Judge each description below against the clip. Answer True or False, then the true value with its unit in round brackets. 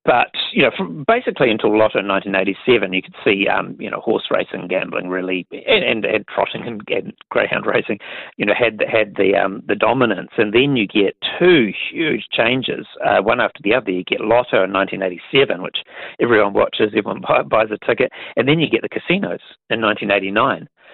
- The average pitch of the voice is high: False (95 Hz)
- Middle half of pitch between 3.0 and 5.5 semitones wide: False (2.6 semitones)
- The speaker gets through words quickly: True (210 wpm)